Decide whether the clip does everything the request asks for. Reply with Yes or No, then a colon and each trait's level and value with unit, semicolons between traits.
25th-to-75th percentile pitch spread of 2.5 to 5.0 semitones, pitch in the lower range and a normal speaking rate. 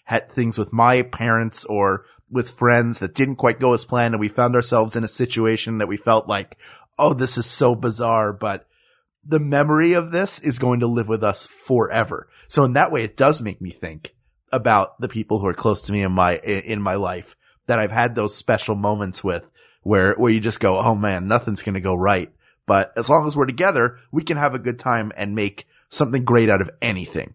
No: average, 3.1 semitones; low, 115 Hz; fast, 225 wpm